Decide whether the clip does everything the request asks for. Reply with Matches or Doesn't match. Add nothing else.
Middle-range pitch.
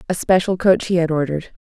Matches